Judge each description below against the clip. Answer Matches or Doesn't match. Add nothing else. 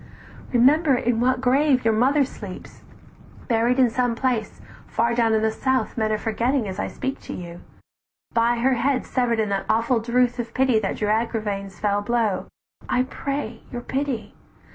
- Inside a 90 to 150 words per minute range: Doesn't match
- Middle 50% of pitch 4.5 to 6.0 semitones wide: Doesn't match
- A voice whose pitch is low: Doesn't match